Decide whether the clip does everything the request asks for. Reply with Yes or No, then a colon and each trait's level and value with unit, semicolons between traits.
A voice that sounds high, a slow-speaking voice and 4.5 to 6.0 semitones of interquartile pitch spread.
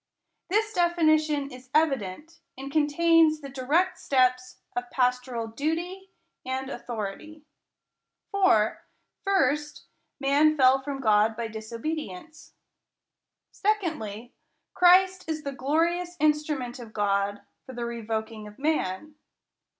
Yes: very high, 275 Hz; slow, 115 wpm; average, 5.2 semitones